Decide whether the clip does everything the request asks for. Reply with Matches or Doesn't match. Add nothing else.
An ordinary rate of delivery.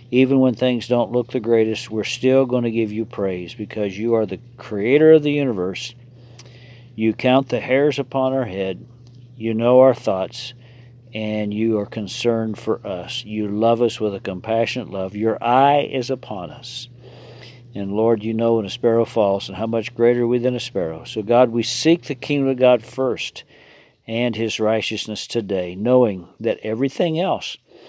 Matches